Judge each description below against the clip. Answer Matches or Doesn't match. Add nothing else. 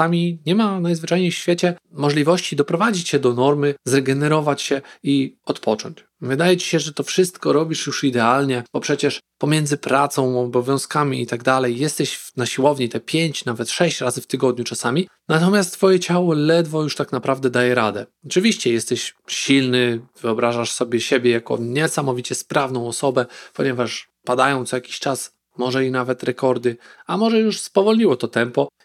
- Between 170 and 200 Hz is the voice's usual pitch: Doesn't match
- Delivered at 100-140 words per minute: Doesn't match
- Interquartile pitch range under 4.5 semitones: Doesn't match